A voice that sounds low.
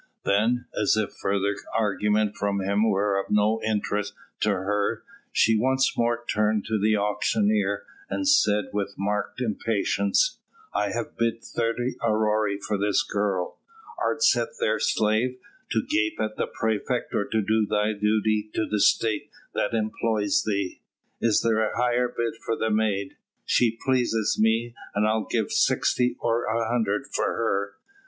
Yes: low, 110 Hz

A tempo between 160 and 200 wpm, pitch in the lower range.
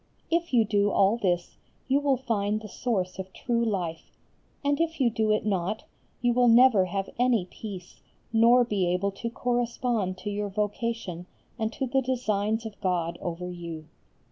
No: average, 170 wpm; high, 215 Hz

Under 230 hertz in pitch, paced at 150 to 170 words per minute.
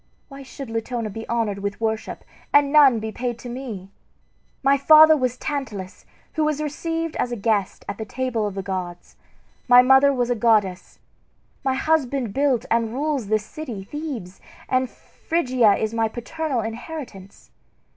No: high, 245 Hz; average, 160 wpm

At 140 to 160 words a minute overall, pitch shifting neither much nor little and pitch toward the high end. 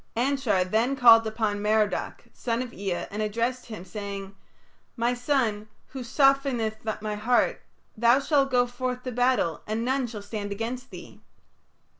Yes: average, 150 wpm; average, 3.1 semitones; high, 230 Hz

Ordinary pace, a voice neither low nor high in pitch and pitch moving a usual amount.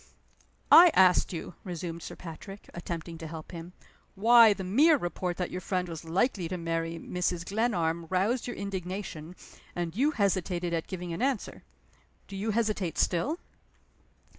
Yes: average, 155 wpm; medium, 180 Hz; average, 3.5 semitones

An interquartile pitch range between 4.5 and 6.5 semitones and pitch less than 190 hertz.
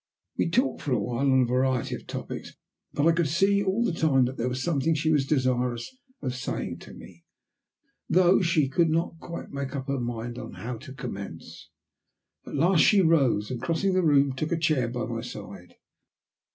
Yes: average, 5.1 semitones; low, 135 Hz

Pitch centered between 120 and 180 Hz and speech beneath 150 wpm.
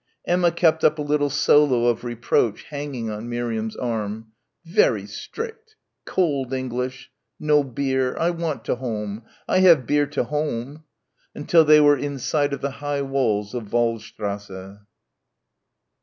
Yes: low, 135 Hz; average, 140 wpm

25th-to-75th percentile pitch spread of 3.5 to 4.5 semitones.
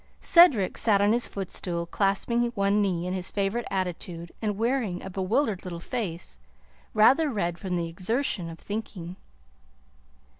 Yes: average, 3.9 semitones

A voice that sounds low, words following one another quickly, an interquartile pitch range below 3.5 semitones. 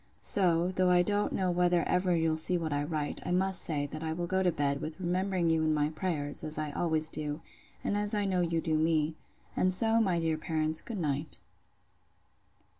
No: medium, 165 Hz; fast, 210 wpm; average, 2.8 semitones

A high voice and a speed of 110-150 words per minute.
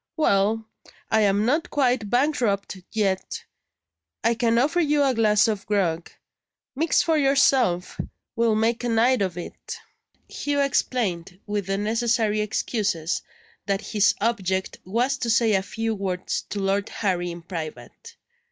Yes: high, 215 Hz; average, 145 wpm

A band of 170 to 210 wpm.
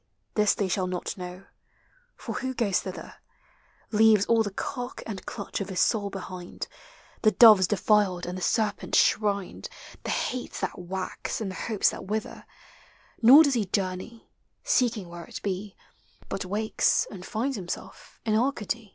No: average, 160 wpm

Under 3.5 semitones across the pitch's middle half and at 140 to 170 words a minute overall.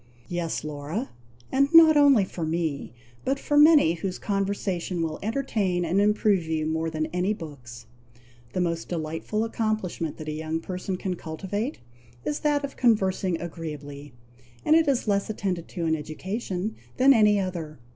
No: average, 5.2 semitones; average, 155 wpm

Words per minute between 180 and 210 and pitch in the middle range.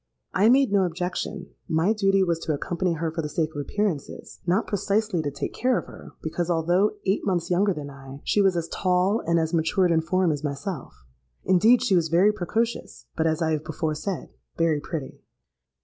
Yes: average, 195 wpm; medium, 175 Hz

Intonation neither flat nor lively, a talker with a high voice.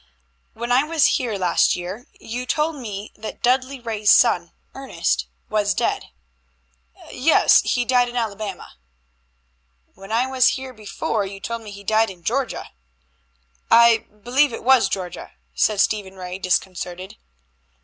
Yes: average, 4.2 semitones; high, 225 Hz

